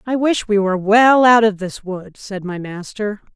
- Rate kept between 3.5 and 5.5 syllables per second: Yes, 4.5 syllables/s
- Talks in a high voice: Yes, high, 205 Hz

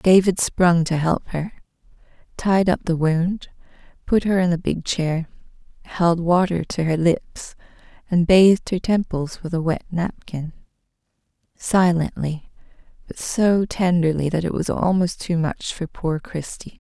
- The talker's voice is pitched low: No, medium, 170 Hz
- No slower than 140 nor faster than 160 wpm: Yes, average, 145 wpm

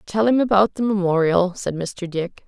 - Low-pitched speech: No, high, 190 Hz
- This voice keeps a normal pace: Yes, average, 195 wpm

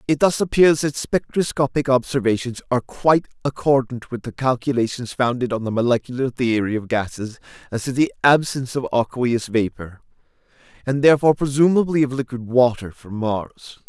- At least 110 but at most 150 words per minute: Yes, average, 145 wpm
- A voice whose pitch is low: Yes, low, 130 Hz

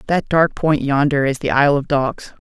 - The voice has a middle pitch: Yes, medium, 145 Hz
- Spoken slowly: No, fast, 220 wpm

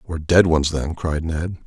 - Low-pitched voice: Yes, very low, 80 Hz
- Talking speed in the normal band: No, fast, 215 wpm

